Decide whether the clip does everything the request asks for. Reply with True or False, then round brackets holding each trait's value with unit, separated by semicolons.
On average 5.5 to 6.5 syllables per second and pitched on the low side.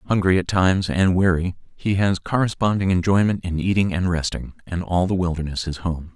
False (5.3 syllables/s; 90 Hz)